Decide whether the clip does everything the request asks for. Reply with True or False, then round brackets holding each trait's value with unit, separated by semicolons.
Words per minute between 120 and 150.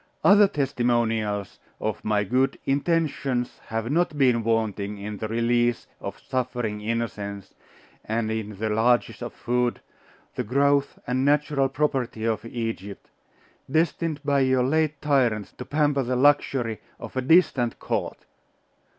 True (135 wpm)